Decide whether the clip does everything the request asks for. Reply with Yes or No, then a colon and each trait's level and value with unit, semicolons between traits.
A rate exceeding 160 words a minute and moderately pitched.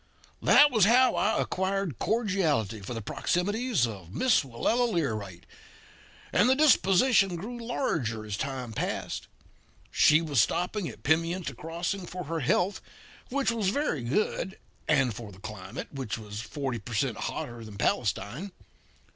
No: average, 145 wpm; medium, 160 Hz